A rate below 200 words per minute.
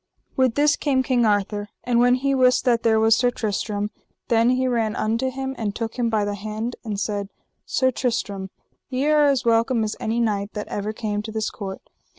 No: fast, 205 wpm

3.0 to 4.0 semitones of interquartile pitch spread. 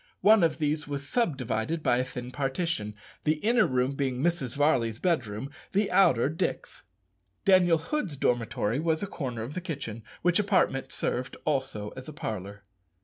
No: wide, 5.4 semitones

